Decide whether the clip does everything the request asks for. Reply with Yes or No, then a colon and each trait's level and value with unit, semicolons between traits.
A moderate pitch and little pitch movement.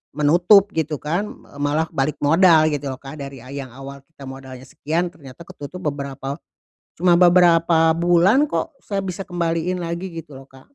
No: medium, 160 Hz; average, 4.1 semitones